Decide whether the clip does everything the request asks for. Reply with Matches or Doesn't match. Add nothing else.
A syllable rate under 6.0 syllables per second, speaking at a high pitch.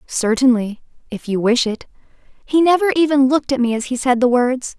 Matches